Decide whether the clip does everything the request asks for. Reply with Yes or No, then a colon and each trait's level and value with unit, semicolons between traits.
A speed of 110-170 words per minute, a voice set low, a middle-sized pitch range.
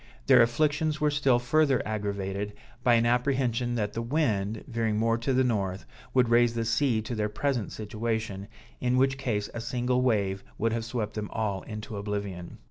No: average, 180 wpm; low, 115 Hz; average, 3.2 semitones